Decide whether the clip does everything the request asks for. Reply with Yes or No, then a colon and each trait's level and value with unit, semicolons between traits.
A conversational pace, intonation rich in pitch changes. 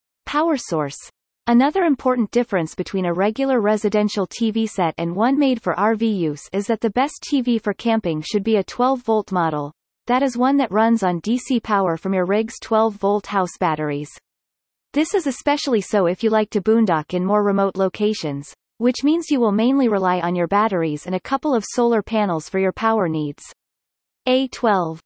No: average, 185 wpm; average, 5.0 semitones